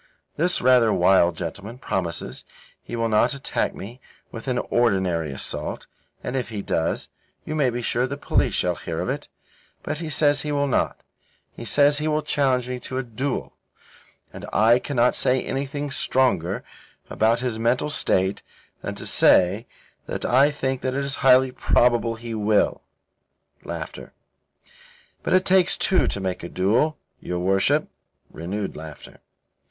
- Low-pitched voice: Yes, low, 120 Hz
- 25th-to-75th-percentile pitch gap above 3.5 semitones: Yes, average, 5.3 semitones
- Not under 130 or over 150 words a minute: No, average, 165 wpm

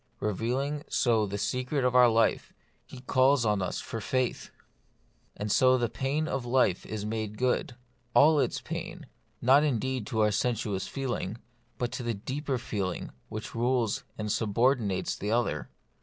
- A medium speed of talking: Yes, average, 160 wpm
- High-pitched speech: No, low, 120 Hz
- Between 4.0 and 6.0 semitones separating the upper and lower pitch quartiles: No, average, 3.4 semitones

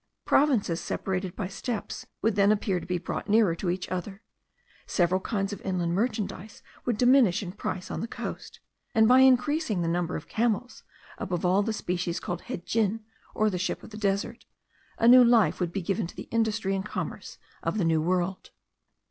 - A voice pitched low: No, high, 200 Hz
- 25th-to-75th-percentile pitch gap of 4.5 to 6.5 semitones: No, average, 3.8 semitones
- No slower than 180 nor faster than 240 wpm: Yes, average, 190 wpm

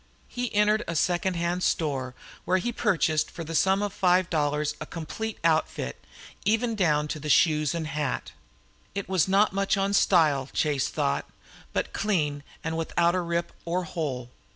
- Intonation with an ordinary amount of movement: Yes, average, 4.1 semitones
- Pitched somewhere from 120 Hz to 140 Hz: No, medium, 170 Hz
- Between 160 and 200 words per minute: Yes, average, 165 wpm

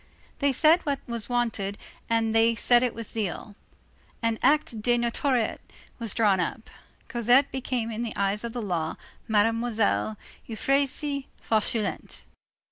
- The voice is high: Yes, high, 230 Hz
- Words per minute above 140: No, slow, 135 wpm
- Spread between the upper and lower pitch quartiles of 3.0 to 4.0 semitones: No, narrow, 2.4 semitones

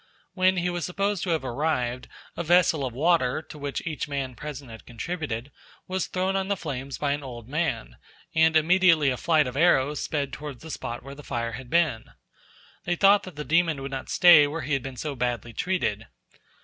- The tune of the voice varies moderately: Yes, average, 4.8 semitones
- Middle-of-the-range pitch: Yes, medium, 150 Hz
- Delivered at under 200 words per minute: No, fast, 205 wpm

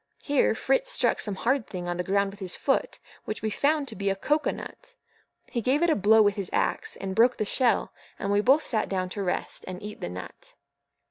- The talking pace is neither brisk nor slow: No, fast, 240 wpm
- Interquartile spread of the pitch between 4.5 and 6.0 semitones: Yes, wide, 5.6 semitones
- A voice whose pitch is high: Yes, high, 210 Hz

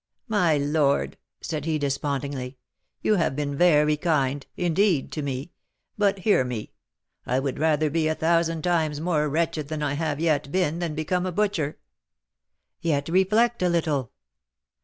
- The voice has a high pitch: No, medium, 155 Hz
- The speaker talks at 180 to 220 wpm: No, average, 155 wpm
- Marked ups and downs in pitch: No, average, 3.1 semitones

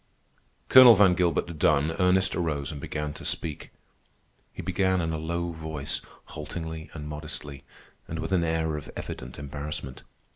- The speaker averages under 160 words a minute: Yes, average, 150 wpm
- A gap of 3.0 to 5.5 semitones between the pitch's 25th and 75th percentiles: No, narrow, 2.4 semitones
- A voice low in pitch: Yes, very low, 80 Hz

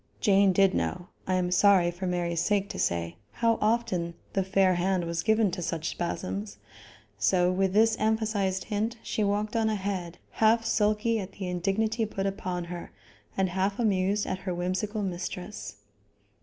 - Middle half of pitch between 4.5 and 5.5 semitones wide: No, average, 3.0 semitones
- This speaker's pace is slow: No, average, 165 wpm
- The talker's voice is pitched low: No, high, 190 Hz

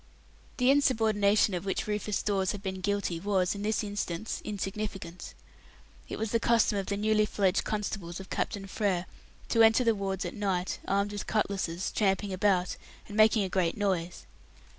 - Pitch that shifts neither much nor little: No, narrow, 2.1 semitones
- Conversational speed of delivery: Yes, average, 170 wpm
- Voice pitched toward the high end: Yes, high, 200 Hz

